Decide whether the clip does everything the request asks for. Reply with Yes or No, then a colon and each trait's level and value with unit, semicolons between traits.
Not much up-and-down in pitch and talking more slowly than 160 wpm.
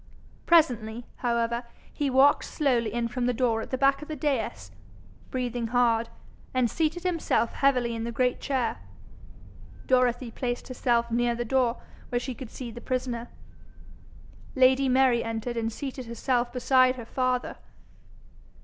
Yes: narrow, 1.9 semitones; average, 150 wpm